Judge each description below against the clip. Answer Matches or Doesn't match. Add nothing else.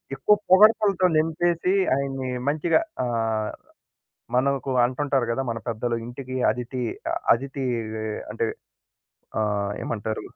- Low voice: Matches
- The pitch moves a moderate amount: Matches